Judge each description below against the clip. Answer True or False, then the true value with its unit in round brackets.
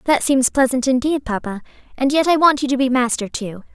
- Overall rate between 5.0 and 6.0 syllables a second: True (5.7 syllables/s)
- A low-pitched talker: False (260 Hz)